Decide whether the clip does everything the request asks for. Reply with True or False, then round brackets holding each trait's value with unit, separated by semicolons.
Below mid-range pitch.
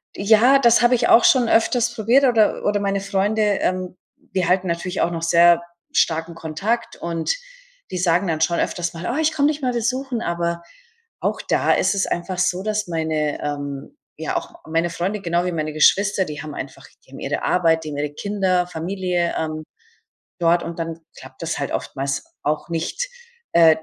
False (180 Hz)